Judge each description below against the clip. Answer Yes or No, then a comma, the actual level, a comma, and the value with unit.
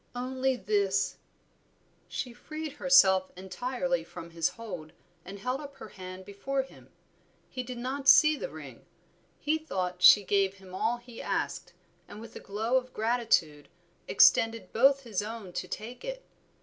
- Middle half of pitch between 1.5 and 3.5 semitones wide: No, wide, 5.5 semitones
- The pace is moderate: Yes, average, 155 wpm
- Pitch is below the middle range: No, high, 230 Hz